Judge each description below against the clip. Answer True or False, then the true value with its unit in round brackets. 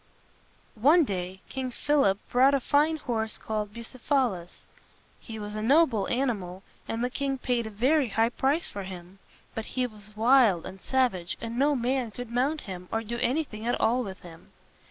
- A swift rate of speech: False (195 wpm)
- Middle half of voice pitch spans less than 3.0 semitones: False (4.2 semitones)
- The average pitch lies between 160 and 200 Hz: False (235 Hz)